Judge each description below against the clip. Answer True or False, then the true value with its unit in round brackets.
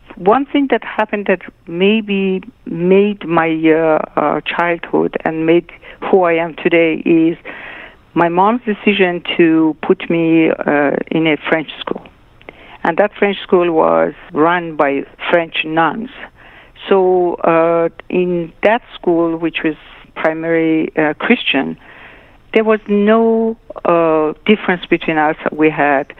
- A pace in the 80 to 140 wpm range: True (135 wpm)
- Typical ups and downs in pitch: True (4.0 semitones)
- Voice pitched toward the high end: False (170 Hz)